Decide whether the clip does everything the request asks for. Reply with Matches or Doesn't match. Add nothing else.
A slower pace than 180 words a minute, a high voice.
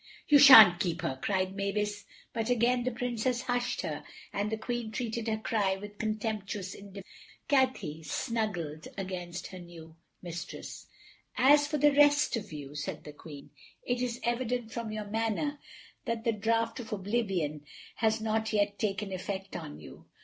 Matches